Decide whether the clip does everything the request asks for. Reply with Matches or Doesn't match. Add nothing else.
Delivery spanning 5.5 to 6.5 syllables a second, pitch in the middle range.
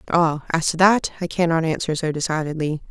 Matches